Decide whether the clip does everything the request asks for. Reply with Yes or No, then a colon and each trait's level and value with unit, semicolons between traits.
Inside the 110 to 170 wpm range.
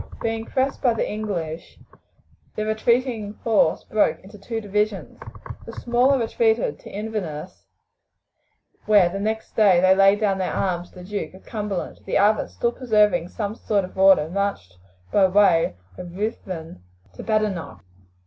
Yes: average, 150 wpm